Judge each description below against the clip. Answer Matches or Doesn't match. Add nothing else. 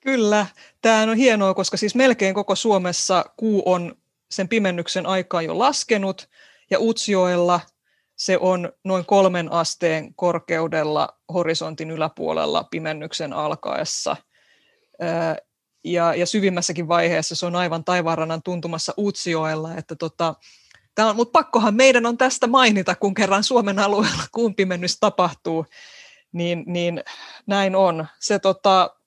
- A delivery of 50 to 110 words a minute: Doesn't match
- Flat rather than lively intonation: Doesn't match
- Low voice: Doesn't match